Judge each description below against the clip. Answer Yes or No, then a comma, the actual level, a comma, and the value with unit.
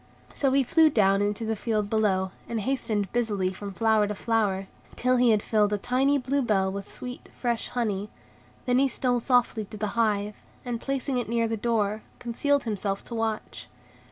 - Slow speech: No, average, 185 wpm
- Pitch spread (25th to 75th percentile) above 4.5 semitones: No, average, 3.2 semitones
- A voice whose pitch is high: Yes, high, 225 Hz